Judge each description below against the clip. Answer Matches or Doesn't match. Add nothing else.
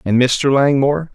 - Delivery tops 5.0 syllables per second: Doesn't match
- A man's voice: Matches